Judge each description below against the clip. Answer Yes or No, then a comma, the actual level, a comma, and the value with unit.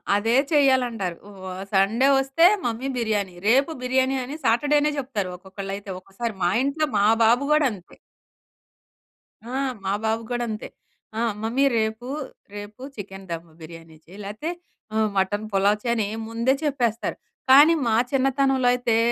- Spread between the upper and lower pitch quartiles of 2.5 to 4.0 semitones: No, average, 4.7 semitones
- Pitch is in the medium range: No, high, 230 Hz